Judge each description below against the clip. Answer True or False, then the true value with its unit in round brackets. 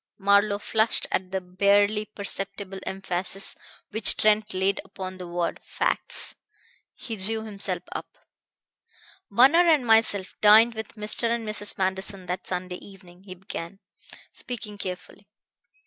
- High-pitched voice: True (200 Hz)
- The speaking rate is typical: False (130 wpm)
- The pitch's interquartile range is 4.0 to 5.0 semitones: False (2.4 semitones)